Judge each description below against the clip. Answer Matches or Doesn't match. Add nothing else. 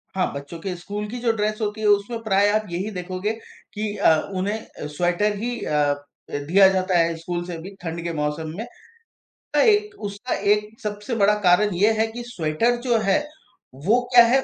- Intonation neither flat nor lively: Matches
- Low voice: Doesn't match